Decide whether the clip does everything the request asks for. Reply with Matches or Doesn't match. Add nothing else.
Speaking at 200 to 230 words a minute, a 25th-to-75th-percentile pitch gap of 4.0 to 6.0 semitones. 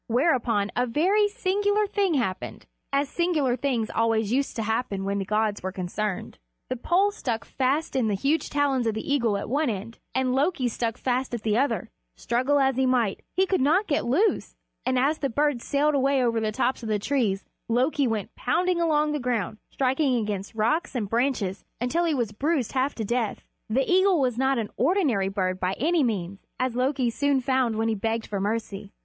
Matches